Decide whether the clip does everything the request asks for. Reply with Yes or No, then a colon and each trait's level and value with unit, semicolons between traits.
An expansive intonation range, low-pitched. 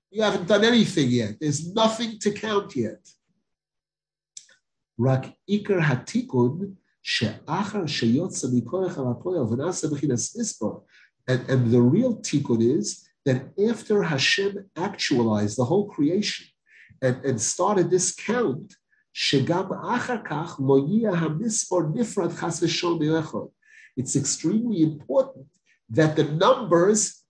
No: wide, 7.5 semitones; medium, 175 Hz